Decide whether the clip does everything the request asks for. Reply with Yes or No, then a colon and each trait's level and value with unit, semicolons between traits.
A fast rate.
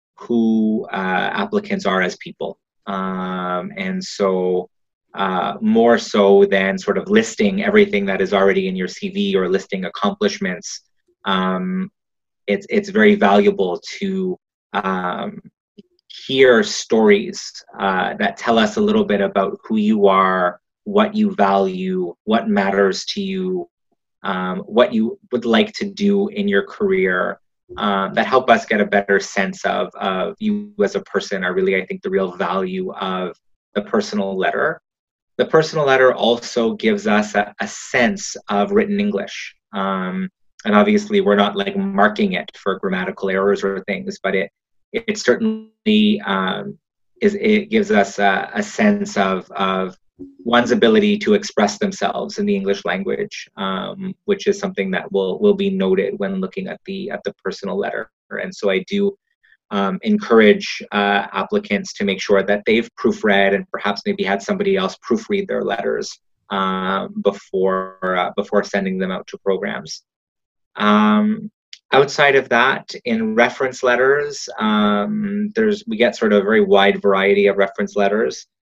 Yes: fast, 155 wpm